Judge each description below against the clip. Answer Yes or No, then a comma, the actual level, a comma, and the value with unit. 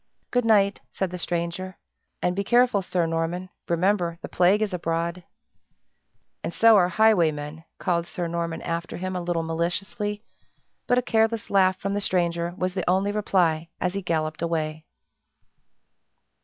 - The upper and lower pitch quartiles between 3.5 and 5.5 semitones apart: No, average, 2.9 semitones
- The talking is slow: No, average, 155 wpm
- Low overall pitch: No, medium, 180 Hz